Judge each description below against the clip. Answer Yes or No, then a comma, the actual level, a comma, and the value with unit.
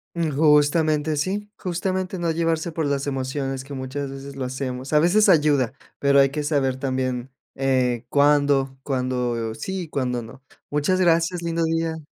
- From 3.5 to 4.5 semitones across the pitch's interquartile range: Yes, average, 3.8 semitones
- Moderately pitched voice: Yes, medium, 145 Hz